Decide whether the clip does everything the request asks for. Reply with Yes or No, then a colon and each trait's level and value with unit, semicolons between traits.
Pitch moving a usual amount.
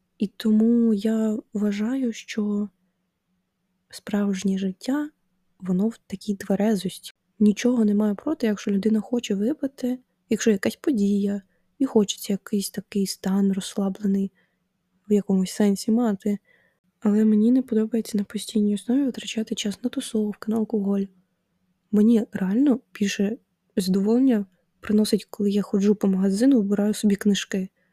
No: narrow, 2.3 semitones